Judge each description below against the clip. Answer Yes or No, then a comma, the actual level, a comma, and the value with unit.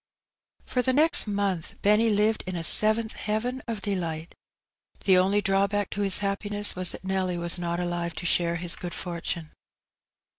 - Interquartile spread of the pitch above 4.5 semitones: No, average, 3.2 semitones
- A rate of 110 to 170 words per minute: Yes, average, 165 wpm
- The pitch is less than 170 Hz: No, high, 195 Hz